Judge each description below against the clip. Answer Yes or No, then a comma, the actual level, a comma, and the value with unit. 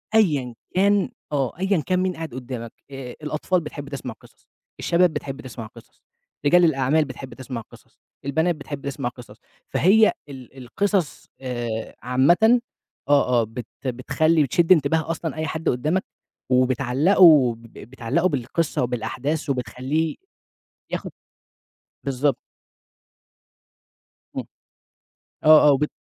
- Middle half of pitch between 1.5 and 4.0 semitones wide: No, average, 4.5 semitones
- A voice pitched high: No, medium, 140 Hz